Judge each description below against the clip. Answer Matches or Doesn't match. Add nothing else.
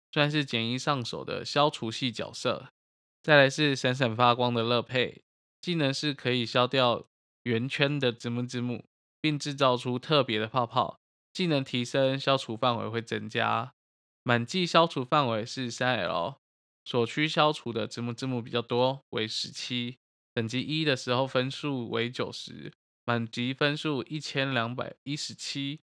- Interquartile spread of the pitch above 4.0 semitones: Doesn't match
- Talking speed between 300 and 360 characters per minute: Doesn't match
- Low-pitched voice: Matches